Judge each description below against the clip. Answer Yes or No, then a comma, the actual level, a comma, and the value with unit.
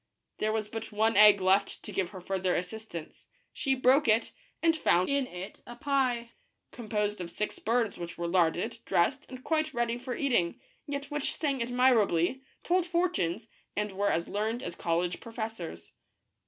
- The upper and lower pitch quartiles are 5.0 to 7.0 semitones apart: Yes, wide, 5.6 semitones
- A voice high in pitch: Yes, high, 220 Hz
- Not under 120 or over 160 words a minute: No, average, 170 wpm